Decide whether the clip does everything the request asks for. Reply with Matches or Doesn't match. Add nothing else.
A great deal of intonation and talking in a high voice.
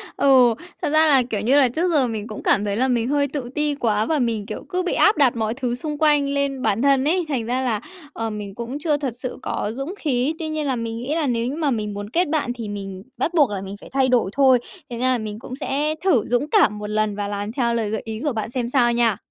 Doesn't match